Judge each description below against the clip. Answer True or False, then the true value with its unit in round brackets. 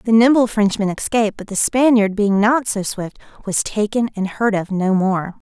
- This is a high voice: True (210 Hz)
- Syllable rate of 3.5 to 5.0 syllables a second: True (4.8 syllables/s)